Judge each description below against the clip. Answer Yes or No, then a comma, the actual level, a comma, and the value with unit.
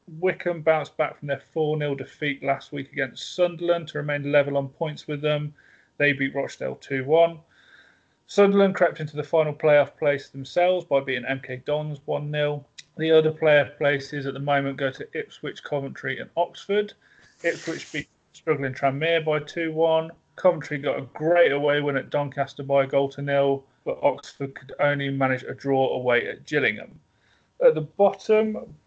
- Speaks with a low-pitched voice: No, medium, 150 Hz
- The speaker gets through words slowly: No, average, 175 wpm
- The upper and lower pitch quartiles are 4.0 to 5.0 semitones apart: No, average, 2.8 semitones